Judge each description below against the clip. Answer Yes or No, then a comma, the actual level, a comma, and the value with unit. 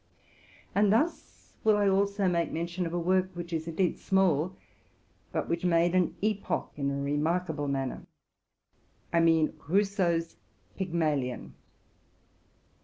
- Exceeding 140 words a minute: No, slow, 135 wpm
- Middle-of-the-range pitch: Yes, medium, 170 Hz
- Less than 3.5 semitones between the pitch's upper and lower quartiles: Yes, average, 3.0 semitones